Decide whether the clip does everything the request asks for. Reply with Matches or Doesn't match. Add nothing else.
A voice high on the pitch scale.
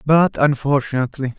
Doesn't match